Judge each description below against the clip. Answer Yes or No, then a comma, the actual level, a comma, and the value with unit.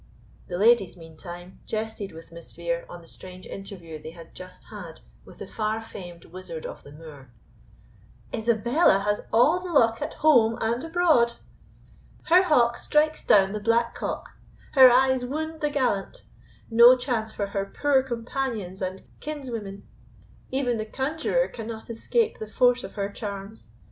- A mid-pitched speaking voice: No, high, 225 Hz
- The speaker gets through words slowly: No, average, 155 wpm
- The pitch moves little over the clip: No, average, 5.3 semitones